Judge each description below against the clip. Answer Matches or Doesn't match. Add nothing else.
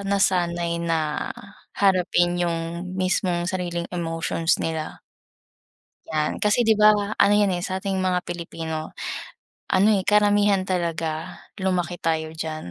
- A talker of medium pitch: Matches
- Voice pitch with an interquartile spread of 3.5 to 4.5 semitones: Doesn't match